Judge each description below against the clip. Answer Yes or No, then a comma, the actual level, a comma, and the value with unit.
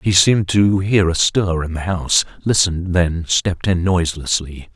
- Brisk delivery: No, average, 150 wpm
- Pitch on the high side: No, very low, 90 Hz